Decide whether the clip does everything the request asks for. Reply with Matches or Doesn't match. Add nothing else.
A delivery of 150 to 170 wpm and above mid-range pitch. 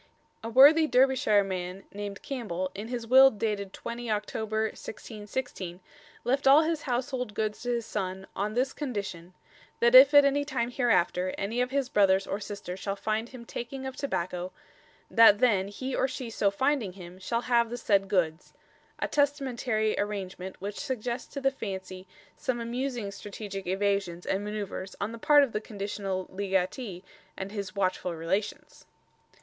Matches